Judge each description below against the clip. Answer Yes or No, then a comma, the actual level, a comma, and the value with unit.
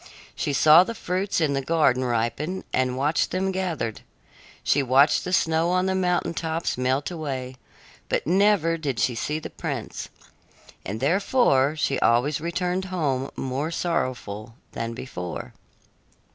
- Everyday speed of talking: Yes, average, 145 wpm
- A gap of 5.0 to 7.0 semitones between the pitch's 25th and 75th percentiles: Yes, wide, 5.6 semitones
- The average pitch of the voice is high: No, medium, 150 Hz